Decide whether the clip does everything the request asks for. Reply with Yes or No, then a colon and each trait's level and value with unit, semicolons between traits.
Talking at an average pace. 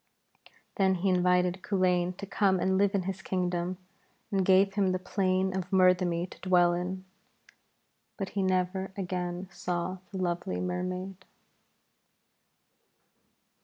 No: slow, 130 wpm